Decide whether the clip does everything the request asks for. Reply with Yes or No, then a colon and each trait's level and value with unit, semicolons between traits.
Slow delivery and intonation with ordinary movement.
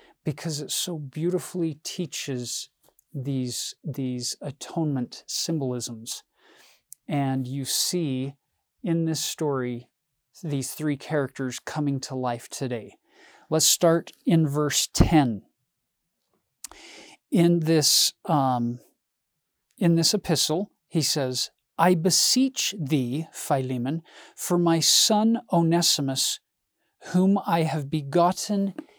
Yes: slow, 95 wpm; average, 4.1 semitones